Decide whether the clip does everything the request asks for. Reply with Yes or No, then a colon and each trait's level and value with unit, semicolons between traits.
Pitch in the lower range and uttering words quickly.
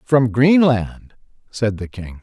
No: low, 120 Hz; slow, 135 wpm